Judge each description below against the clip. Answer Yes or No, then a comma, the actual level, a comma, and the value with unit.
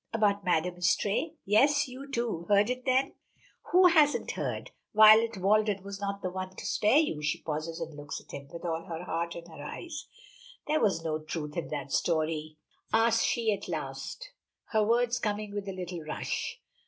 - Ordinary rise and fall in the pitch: No, wide, 5.7 semitones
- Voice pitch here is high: Yes, high, 200 Hz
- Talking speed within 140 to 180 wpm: No, average, 190 wpm